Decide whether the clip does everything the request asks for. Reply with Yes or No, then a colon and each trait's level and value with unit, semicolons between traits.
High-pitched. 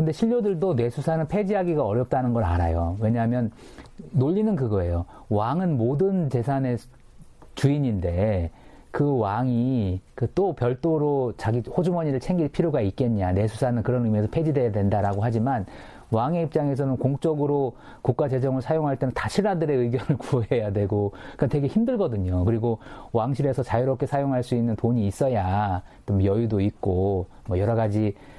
No: low, 125 Hz